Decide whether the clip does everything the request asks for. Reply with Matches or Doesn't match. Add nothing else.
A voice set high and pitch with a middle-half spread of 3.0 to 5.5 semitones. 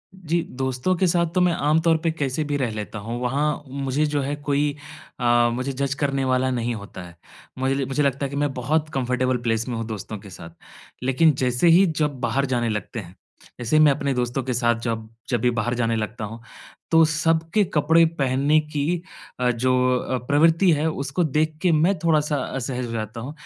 Doesn't match